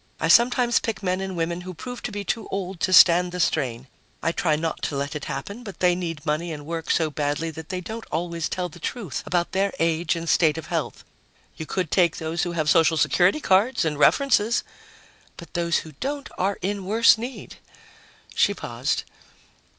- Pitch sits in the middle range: Yes, medium, 175 Hz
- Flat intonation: No, average, 3.5 semitones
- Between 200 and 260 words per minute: Yes, fast, 205 wpm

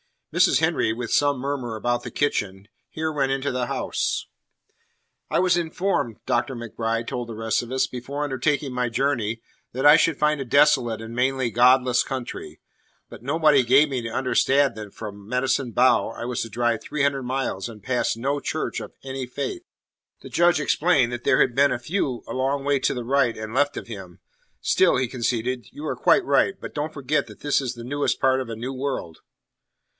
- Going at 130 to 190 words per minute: No, average, 200 wpm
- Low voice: Yes, low, 130 Hz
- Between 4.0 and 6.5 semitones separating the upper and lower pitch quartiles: No, average, 3.2 semitones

